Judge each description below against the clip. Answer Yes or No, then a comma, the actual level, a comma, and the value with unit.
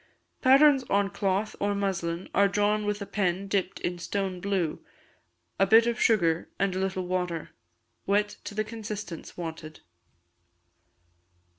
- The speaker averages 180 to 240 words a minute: No, average, 140 wpm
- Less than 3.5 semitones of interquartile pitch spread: Yes, narrow, 2.5 semitones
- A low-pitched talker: No, high, 195 Hz